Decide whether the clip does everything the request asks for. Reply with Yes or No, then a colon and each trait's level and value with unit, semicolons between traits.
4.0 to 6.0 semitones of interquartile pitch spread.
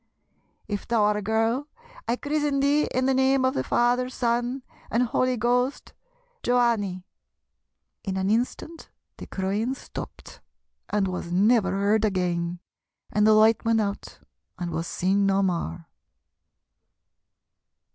Yes: average, 4.4 semitones